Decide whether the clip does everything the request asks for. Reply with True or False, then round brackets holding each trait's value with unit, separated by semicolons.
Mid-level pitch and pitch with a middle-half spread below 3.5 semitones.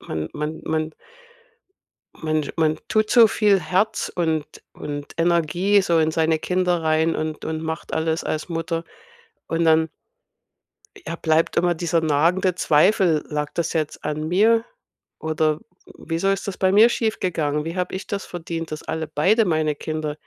True (165 Hz; 2.6 semitones)